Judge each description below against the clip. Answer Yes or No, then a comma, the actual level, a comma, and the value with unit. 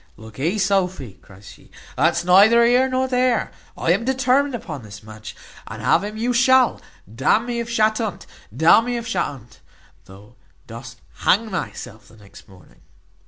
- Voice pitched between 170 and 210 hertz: Yes, high, 190 Hz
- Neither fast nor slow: Yes, average, 175 wpm